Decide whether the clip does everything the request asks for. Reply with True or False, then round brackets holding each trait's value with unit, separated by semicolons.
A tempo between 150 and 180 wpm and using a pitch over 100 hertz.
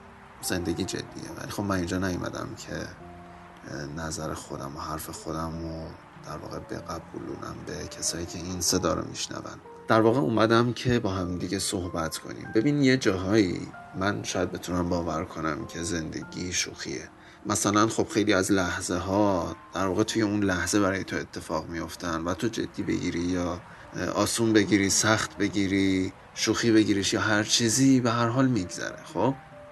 False (155 wpm; 95 Hz)